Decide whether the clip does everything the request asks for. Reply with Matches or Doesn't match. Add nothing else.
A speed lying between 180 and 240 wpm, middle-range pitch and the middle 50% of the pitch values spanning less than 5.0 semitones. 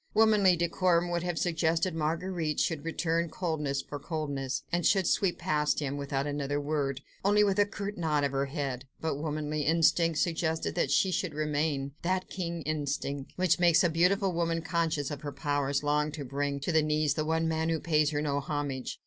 Matches